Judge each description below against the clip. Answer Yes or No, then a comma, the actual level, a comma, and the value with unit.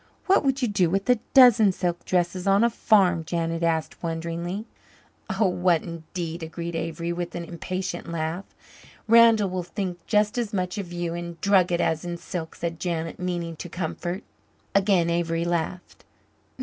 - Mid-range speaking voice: Yes, medium, 175 Hz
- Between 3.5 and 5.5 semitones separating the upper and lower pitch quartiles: No, narrow, 2.6 semitones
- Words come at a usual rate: Yes, average, 160 wpm